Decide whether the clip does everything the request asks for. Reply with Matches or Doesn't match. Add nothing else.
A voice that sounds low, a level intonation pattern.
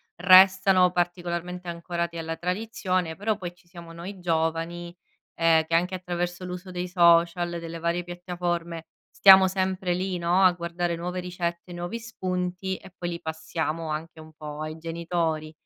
Doesn't match